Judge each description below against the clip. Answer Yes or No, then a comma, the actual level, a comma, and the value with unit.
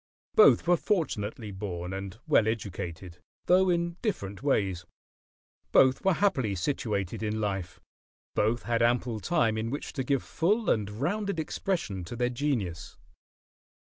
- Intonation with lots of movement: Yes, wide, 8.5 semitones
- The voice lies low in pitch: Yes, low, 115 Hz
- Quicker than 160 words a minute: No, slow, 135 wpm